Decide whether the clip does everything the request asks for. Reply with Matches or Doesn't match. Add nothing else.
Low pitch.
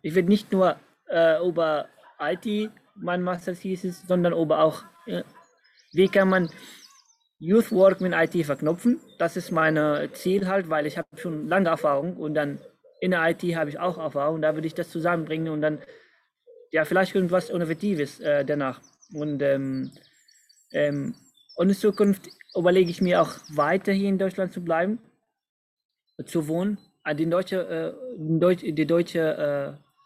Doesn't match